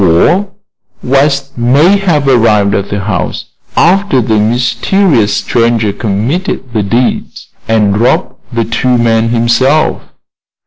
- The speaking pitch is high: No, low, 120 Hz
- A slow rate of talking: Yes, slow, 120 wpm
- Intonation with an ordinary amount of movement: Yes, average, 4.4 semitones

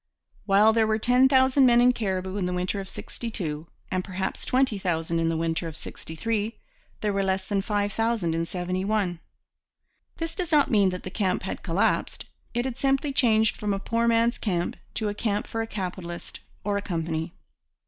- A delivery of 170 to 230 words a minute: Yes, average, 190 wpm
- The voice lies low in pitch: No, high, 200 Hz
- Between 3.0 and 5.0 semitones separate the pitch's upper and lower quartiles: Yes, average, 4.1 semitones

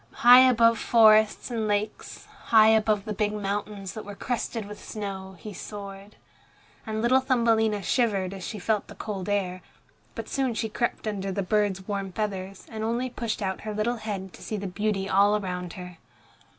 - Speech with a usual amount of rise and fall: No, narrow, 2.2 semitones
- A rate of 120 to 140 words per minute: No, average, 180 wpm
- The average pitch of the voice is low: No, high, 210 Hz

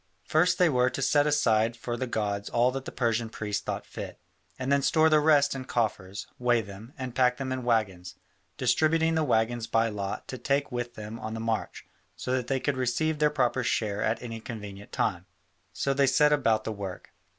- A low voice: Yes, low, 120 Hz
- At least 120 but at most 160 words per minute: No, fast, 205 wpm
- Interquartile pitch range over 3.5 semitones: Yes, average, 3.9 semitones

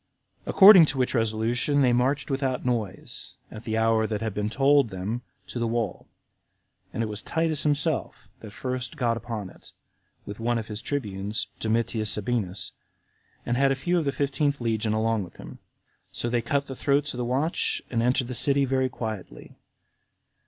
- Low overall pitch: Yes, low, 120 Hz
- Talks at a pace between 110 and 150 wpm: No, average, 180 wpm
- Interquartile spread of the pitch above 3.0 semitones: Yes, average, 3.8 semitones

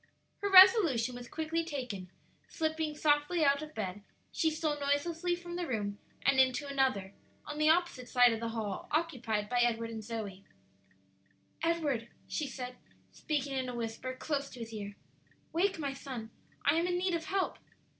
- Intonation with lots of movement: Yes, wide, 5.8 semitones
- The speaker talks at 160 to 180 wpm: Yes, average, 170 wpm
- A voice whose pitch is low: No, very high, 275 Hz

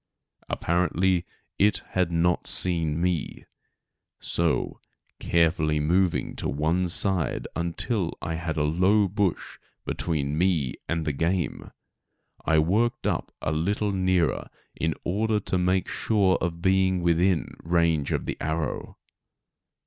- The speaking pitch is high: No, very low, 85 Hz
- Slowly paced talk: Yes, slow, 125 wpm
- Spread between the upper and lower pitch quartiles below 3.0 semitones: Yes, narrow, 2.6 semitones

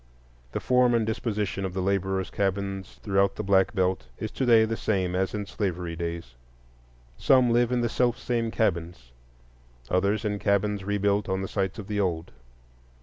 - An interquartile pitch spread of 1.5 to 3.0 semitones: Yes, average, 2.7 semitones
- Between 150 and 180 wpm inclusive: Yes, average, 175 wpm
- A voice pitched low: Yes, low, 100 Hz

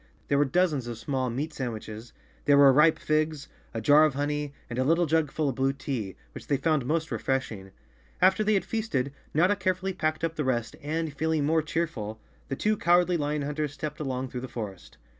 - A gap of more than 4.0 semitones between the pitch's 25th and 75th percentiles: No, average, 3.7 semitones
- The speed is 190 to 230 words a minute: Yes, fast, 205 wpm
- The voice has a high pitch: No, medium, 145 Hz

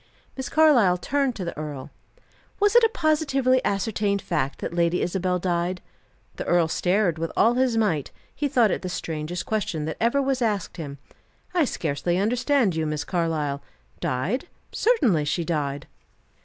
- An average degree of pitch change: No, wide, 7.7 semitones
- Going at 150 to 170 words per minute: Yes, average, 160 wpm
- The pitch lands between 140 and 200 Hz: Yes, medium, 185 Hz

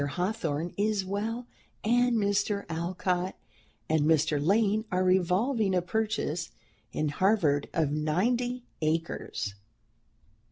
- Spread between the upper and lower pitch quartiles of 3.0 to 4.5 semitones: No, average, 5.0 semitones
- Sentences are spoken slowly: Yes, slow, 105 wpm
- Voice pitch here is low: No, medium, 185 Hz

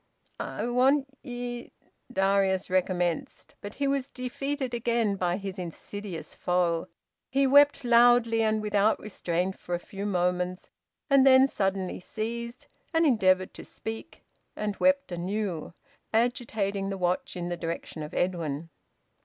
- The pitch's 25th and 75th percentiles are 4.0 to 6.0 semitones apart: Yes, average, 5.1 semitones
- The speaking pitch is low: No, high, 205 Hz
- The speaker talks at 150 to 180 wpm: No, slow, 135 wpm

